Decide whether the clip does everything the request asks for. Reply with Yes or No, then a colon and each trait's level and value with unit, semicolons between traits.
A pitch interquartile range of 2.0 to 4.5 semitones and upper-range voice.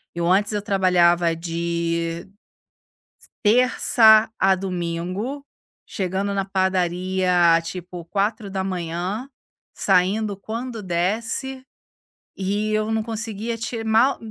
Yes: average, 3.8 semitones; high, 195 Hz